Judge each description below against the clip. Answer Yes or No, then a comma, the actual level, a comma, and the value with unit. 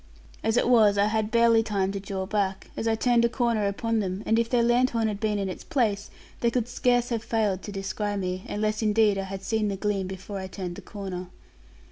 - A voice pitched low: No, high, 210 Hz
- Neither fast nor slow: No, fast, 230 wpm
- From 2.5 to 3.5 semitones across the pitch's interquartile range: Yes, average, 2.8 semitones